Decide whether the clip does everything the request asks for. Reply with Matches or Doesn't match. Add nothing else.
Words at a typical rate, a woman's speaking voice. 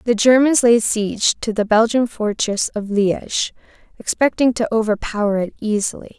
Matches